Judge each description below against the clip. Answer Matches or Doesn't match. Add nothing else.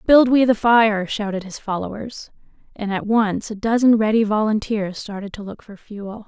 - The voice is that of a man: Doesn't match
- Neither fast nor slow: Matches